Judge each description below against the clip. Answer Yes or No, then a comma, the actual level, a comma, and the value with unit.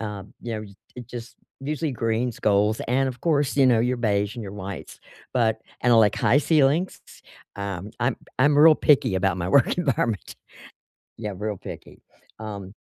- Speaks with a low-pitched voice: Yes, low, 115 Hz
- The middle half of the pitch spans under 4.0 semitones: No, average, 4.6 semitones